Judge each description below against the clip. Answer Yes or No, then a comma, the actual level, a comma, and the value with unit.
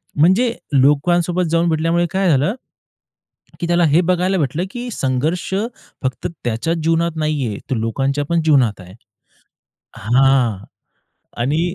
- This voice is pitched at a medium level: Yes, medium, 155 Hz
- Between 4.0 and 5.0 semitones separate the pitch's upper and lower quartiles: Yes, average, 4.5 semitones